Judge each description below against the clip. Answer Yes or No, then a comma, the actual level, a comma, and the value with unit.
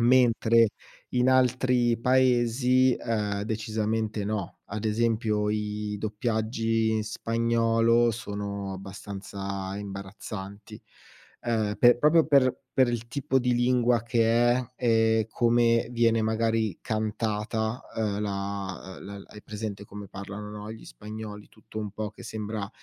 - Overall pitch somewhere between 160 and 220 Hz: No, low, 110 Hz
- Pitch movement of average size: No, narrow, 2.2 semitones